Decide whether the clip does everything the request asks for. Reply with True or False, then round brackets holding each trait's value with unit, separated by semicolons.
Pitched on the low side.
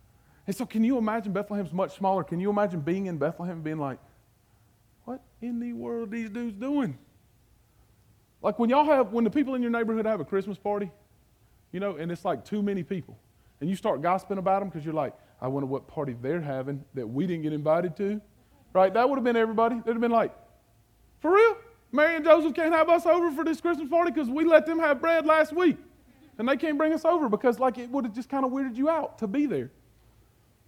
False (205 Hz)